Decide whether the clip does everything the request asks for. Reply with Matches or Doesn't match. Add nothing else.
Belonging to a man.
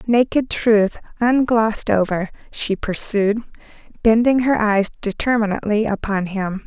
Doesn't match